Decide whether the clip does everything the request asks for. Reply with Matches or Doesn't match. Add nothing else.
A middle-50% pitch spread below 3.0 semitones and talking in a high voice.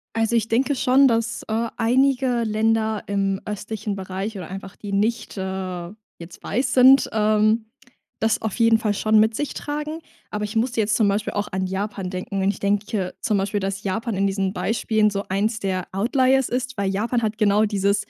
Matches